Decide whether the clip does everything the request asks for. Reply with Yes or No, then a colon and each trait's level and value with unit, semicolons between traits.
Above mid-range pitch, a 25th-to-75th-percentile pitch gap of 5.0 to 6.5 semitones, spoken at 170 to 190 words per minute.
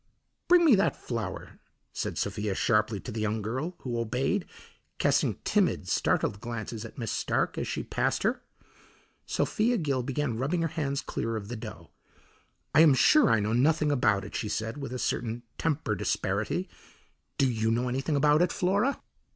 No: low, 125 Hz; wide, 5.5 semitones; average, 175 wpm